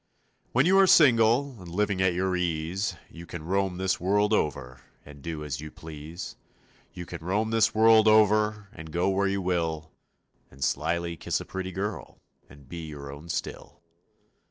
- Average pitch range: Yes, average, 4.6 semitones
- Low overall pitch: Yes, very low, 90 Hz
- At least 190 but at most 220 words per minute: No, average, 175 wpm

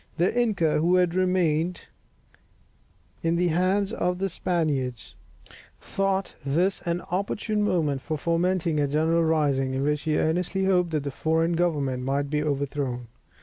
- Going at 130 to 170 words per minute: Yes, average, 150 wpm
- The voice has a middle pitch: Yes, medium, 165 Hz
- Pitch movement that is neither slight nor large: Yes, average, 3.8 semitones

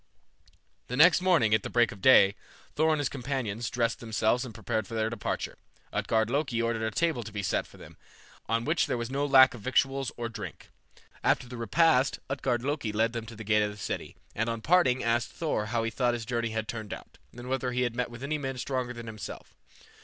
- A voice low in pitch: Yes, low, 120 Hz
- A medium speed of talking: No, fast, 225 wpm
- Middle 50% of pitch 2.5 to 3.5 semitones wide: Yes, average, 3.0 semitones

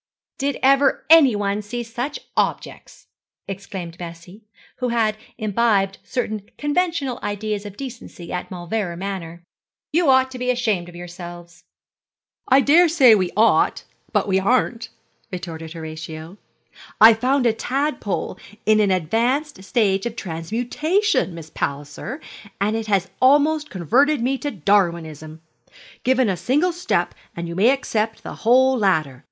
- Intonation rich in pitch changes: Yes, wide, 6.6 semitones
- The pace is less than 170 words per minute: Yes, slow, 135 wpm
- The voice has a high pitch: Yes, high, 215 Hz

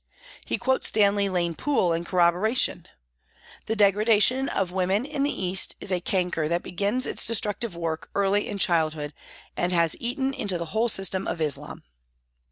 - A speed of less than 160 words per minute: No, average, 170 wpm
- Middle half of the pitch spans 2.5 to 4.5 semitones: Yes, average, 4.2 semitones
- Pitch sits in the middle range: No, high, 195 Hz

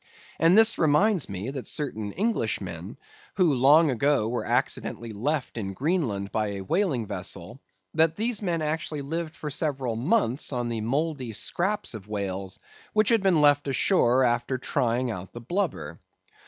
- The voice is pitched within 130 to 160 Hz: Yes, low, 135 Hz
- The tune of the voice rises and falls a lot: Yes, wide, 6.6 semitones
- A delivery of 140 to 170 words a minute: Yes, average, 155 wpm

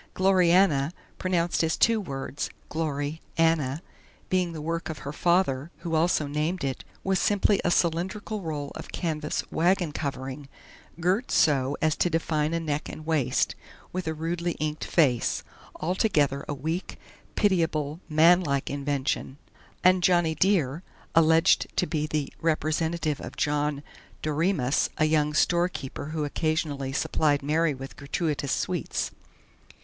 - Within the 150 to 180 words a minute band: No, slow, 135 wpm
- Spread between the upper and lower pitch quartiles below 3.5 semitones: Yes, average, 3.1 semitones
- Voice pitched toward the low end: No, medium, 160 Hz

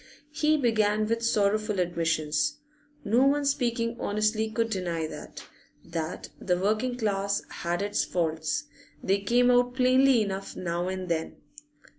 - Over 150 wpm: No, slow, 135 wpm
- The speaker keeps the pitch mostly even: No, average, 5.2 semitones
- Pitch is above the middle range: Yes, high, 215 Hz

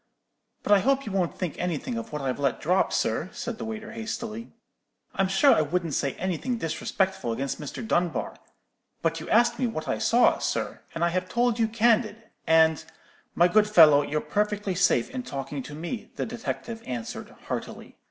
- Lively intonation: Yes, wide, 6.2 semitones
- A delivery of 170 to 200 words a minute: Yes, average, 190 wpm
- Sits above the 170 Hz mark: Yes, high, 190 Hz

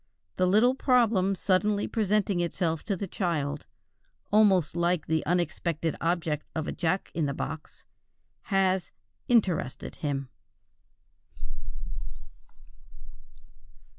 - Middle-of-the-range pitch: Yes, medium, 180 Hz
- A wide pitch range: No, average, 3.8 semitones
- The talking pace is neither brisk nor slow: No, slow, 100 wpm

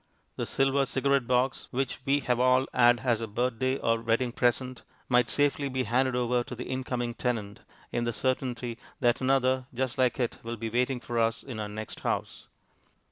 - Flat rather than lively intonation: Yes, narrow, 1.8 semitones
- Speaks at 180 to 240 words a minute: Yes, average, 190 wpm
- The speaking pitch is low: Yes, low, 125 Hz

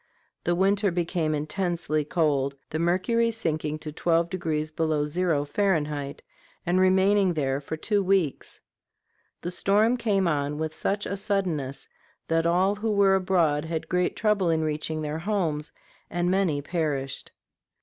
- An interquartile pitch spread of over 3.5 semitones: Yes, average, 4.0 semitones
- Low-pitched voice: No, medium, 170 Hz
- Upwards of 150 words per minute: No, average, 140 wpm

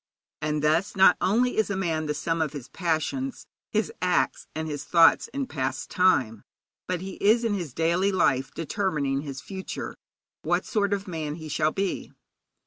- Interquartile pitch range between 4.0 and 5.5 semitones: Yes, average, 4.6 semitones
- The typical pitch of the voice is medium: Yes, medium, 170 Hz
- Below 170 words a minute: No, average, 175 wpm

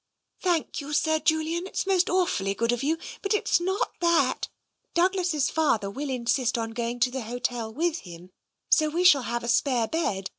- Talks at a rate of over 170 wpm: Yes, average, 190 wpm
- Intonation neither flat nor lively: No, wide, 6.4 semitones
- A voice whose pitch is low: No, very high, 290 Hz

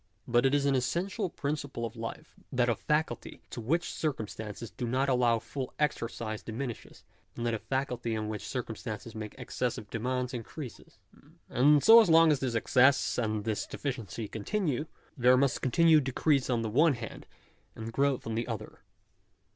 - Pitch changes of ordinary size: Yes, average, 3.8 semitones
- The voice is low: Yes, low, 125 Hz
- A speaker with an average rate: Yes, average, 165 wpm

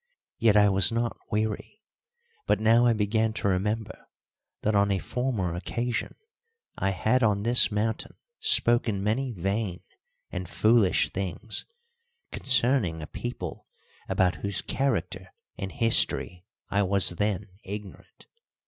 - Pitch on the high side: No, low, 105 Hz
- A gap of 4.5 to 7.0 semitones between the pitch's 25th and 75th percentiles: No, average, 3.1 semitones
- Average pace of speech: No, slow, 125 wpm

